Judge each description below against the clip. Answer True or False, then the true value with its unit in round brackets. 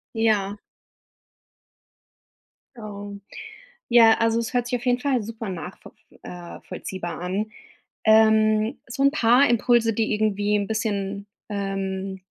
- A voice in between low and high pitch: False (215 Hz)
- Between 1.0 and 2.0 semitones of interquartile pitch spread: False (2.5 semitones)